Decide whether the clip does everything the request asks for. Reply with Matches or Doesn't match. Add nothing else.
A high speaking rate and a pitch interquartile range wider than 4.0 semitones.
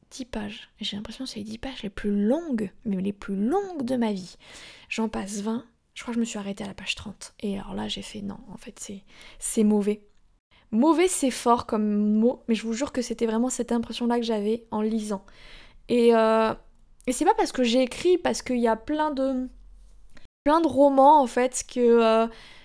Doesn't match